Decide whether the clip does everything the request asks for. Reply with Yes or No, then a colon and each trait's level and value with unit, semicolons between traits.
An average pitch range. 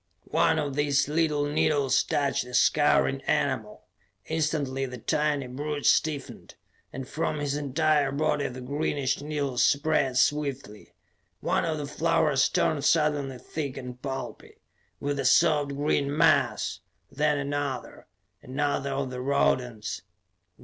No: narrow, 2.0 semitones